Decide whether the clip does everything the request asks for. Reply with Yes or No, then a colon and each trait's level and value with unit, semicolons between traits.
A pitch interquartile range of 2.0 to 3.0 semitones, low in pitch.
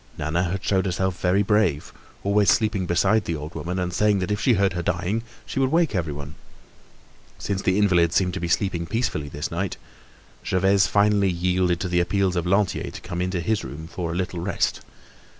Yes: narrow, 2.6 semitones; very low, 90 Hz